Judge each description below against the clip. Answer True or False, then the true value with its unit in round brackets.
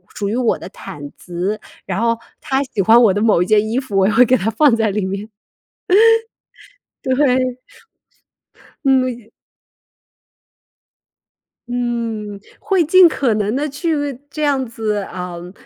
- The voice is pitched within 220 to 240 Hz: True (225 Hz)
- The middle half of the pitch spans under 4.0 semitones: False (4.3 semitones)